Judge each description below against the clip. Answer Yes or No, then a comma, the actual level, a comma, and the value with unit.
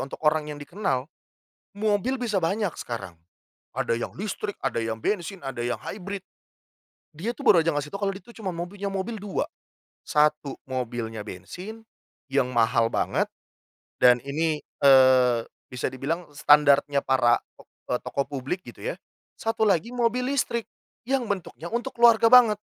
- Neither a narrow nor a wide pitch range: No, wide, 7.8 semitones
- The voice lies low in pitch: No, medium, 165 Hz